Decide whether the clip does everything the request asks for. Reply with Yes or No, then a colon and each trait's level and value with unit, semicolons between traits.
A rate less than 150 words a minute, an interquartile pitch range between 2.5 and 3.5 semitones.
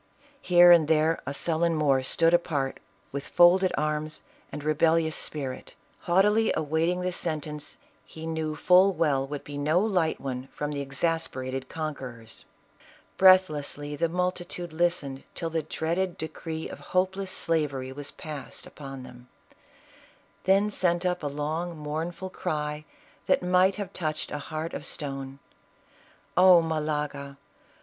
Yes: average, 140 wpm; average, 3.2 semitones